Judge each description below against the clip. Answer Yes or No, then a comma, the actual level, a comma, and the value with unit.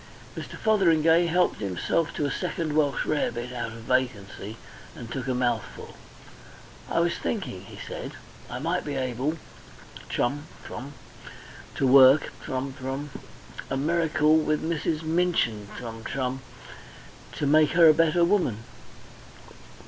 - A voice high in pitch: No, medium, 145 Hz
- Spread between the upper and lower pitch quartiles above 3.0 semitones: Yes, average, 4.6 semitones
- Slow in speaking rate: Yes, slow, 130 wpm